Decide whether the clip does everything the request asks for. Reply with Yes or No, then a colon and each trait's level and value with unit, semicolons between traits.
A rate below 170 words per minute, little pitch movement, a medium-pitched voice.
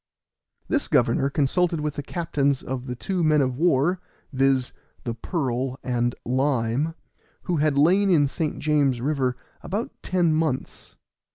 No: average, 145 wpm; average, 3.9 semitones; medium, 145 Hz